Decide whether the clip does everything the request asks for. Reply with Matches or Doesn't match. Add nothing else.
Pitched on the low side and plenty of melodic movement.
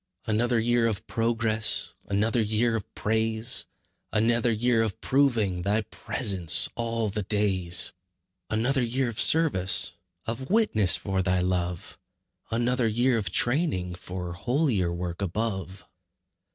Doesn't match